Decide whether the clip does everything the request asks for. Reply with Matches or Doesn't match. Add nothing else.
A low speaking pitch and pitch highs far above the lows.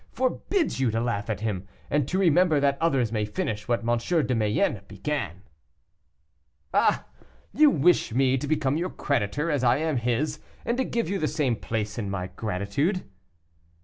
Matches